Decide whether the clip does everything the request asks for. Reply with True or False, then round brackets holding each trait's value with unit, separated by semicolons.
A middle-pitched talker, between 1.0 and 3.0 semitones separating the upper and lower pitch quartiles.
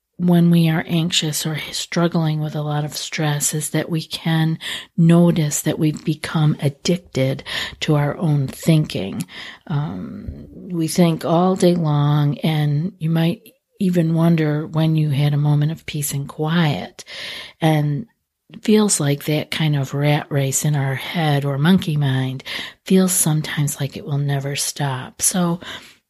True (155 Hz; 2.6 semitones)